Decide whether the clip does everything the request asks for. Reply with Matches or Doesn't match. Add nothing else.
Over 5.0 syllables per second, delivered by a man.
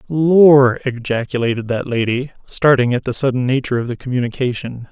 Matches